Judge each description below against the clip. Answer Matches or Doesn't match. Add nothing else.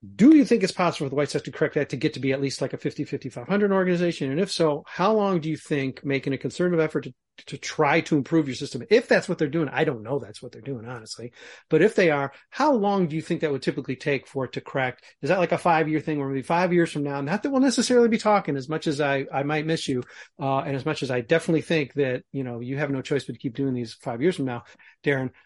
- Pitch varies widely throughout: Doesn't match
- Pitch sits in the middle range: Matches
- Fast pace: Matches